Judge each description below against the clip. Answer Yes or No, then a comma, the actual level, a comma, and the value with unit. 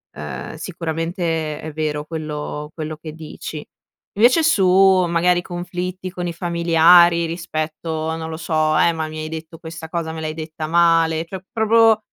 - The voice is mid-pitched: Yes, medium, 165 Hz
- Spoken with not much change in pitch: Yes, narrow, 1.9 semitones